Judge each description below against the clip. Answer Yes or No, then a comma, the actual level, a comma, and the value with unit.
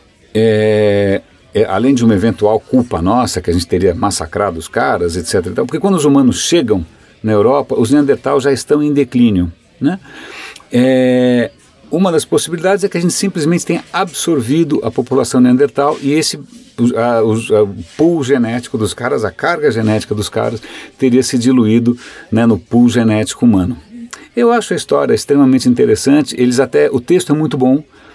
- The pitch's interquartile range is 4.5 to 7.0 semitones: Yes, average, 5.2 semitones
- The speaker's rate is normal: Yes, average, 175 wpm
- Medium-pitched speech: No, low, 125 Hz